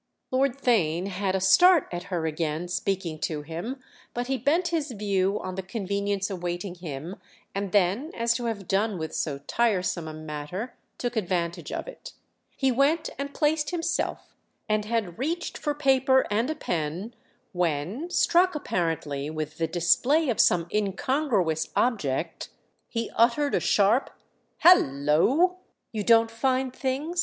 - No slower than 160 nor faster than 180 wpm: No, average, 150 wpm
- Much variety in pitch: Yes, wide, 7.3 semitones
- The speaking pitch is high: Yes, high, 205 Hz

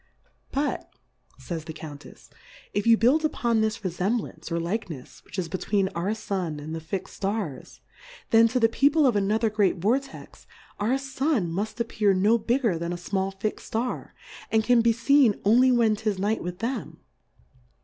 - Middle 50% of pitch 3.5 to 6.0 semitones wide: Yes, average, 4.1 semitones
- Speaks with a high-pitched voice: Yes, high, 215 Hz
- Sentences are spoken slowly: No, average, 170 wpm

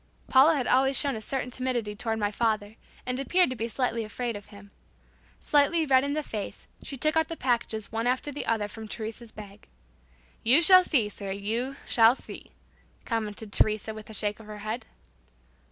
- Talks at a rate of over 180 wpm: Yes, average, 190 wpm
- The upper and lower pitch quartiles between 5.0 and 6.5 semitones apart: No, average, 3.8 semitones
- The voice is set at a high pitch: Yes, high, 230 Hz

